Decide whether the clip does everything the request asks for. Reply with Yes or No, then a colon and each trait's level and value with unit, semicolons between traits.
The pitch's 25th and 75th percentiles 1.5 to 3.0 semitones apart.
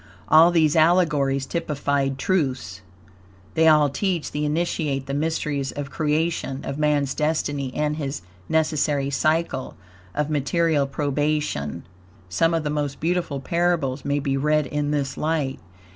Yes: narrow, 2.5 semitones